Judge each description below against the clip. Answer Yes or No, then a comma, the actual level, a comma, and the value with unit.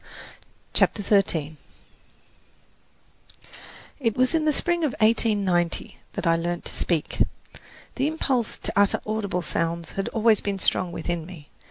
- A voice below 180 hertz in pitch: No, high, 200 Hz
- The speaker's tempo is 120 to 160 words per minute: Yes, slow, 135 wpm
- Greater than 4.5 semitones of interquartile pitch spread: Yes, average, 5.1 semitones